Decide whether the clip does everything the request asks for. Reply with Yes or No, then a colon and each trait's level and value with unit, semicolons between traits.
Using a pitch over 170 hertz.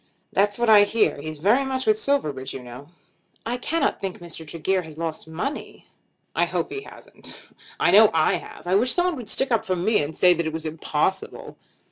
Yes: high, 190 Hz